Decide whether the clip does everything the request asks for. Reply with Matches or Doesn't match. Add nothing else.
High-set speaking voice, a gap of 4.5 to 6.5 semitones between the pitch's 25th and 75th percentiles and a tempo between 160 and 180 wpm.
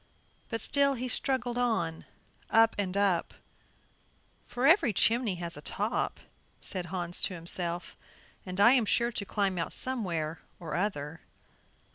Doesn't match